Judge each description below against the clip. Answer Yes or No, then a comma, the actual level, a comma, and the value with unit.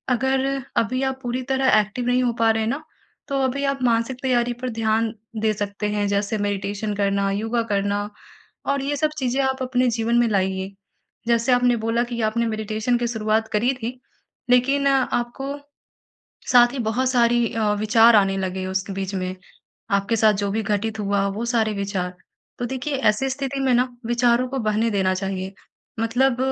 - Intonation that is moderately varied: Yes, average, 3.5 semitones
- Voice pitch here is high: Yes, high, 230 Hz